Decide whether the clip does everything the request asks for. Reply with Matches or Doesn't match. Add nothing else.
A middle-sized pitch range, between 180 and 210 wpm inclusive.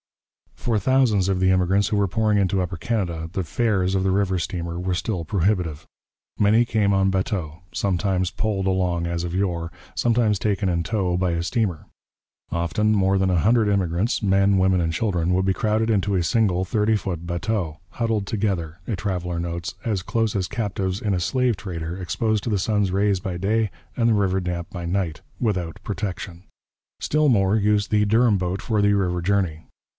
Matches